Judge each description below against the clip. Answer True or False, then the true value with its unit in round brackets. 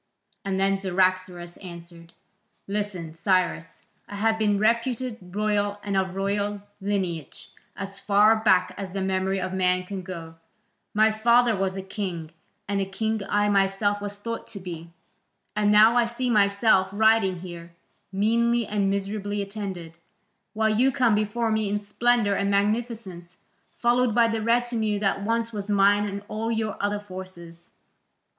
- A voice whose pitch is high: True (205 Hz)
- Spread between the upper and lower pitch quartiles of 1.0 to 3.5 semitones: True (2.5 semitones)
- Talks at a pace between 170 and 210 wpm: False (150 wpm)